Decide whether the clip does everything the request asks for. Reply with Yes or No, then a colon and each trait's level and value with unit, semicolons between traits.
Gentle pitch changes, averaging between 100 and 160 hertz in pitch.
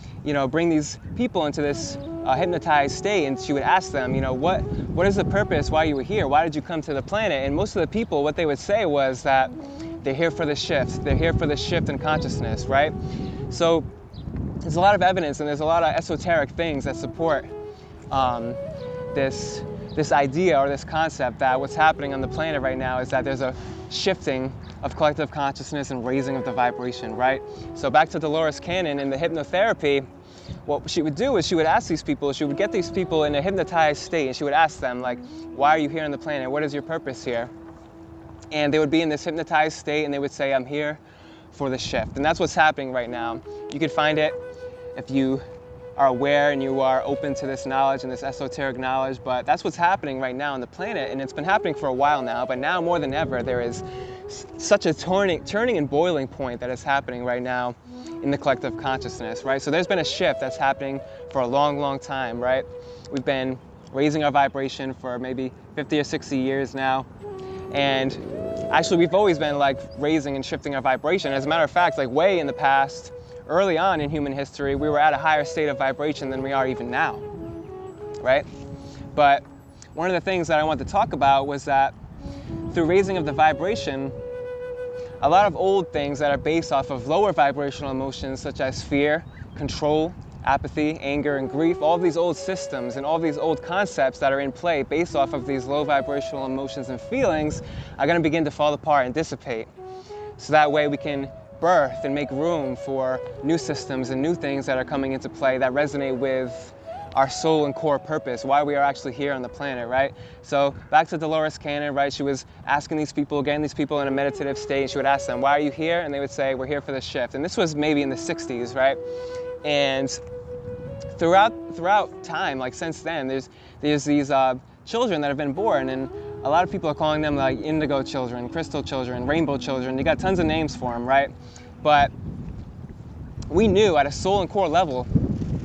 No: average, 3.1 semitones; medium, 140 Hz